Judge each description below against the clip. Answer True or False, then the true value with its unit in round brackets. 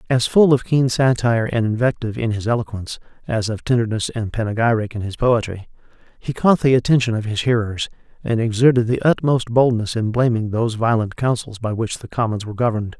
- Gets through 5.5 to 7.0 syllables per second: True (6.0 syllables/s)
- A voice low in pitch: True (115 Hz)